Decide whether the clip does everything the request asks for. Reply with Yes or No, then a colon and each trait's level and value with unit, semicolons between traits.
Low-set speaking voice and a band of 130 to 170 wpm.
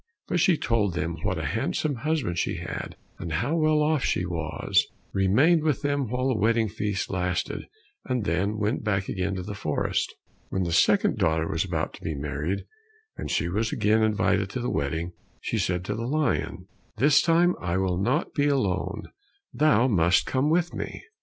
No: low, 105 Hz; average, 185 wpm